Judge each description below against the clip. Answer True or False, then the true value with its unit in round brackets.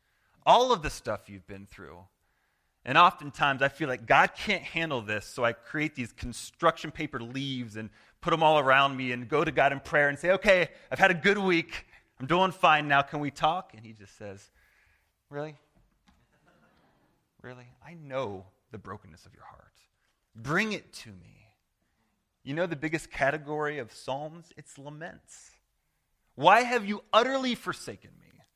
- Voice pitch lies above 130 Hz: True (140 Hz)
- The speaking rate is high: False (170 wpm)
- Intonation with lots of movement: True (6.9 semitones)